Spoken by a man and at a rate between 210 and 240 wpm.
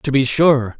Yes: male; fast, 225 wpm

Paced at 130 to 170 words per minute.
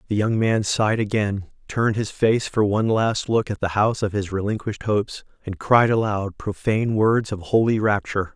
No: average, 185 wpm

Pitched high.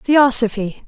Yes: high, 240 Hz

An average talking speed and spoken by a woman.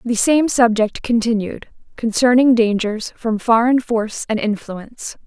No: slow, 125 wpm; female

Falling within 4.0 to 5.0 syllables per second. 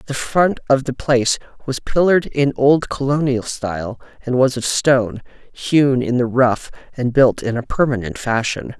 Yes: 4.7 syllables/s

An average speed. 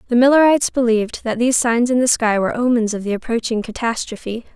Yes: average, 195 wpm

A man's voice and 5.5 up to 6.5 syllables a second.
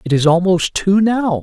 No: male; 4.5 syllables/s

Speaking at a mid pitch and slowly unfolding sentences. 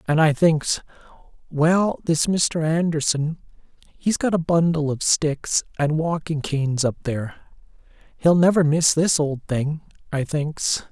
Yes: medium, 155 Hz; slow, 130 wpm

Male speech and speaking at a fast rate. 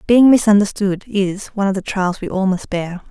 No: female; fast, 210 wpm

